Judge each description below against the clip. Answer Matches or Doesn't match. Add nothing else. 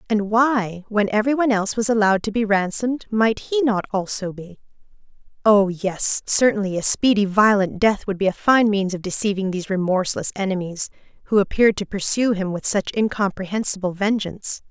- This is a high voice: Matches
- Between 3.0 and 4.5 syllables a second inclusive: Doesn't match